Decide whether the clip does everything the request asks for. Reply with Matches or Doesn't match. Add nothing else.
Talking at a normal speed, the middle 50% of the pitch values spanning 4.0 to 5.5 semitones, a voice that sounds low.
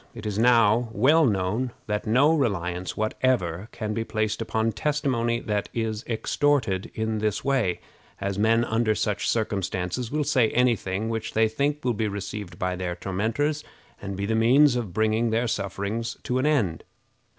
Doesn't match